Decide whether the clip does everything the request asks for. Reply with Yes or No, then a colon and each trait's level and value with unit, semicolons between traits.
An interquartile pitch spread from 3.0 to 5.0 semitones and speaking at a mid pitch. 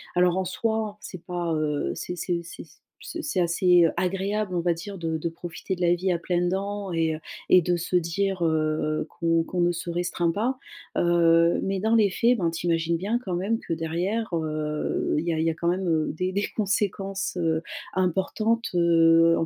No: narrow, 2.6 semitones; medium, 175 Hz